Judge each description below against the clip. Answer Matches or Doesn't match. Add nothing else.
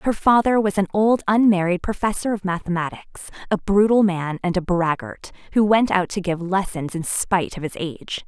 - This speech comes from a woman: Matches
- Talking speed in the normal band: Matches